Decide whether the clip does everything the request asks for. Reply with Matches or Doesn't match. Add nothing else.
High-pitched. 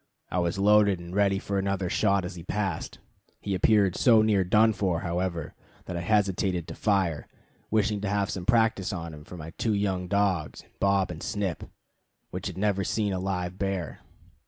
Doesn't match